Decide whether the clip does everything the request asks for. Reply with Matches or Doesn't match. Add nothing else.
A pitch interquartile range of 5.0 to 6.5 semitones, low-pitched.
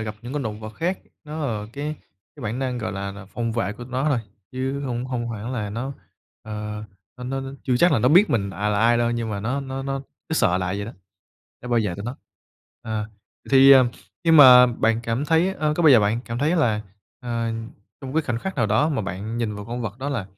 Doesn't match